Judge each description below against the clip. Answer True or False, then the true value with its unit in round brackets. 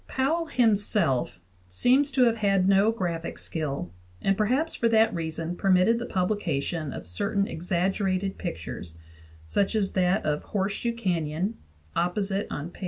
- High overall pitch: True (195 Hz)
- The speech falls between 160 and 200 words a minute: False (145 wpm)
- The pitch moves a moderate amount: True (4.7 semitones)